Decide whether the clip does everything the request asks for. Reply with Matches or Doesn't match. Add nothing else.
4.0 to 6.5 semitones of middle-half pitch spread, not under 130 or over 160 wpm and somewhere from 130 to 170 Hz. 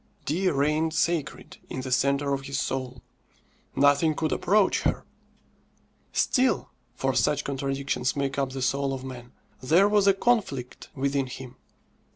Doesn't match